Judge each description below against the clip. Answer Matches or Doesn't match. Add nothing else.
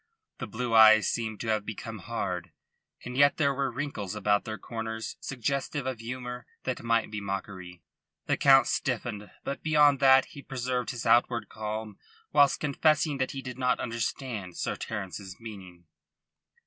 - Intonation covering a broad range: Doesn't match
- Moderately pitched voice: Doesn't match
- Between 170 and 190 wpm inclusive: Doesn't match